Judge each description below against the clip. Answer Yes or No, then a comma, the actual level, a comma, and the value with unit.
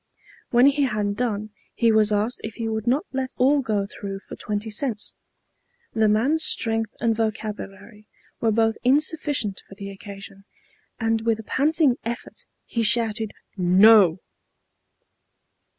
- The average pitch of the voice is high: Yes, high, 225 Hz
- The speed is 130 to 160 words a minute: Yes, average, 140 wpm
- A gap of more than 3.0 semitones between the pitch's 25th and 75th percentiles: No, average, 2.7 semitones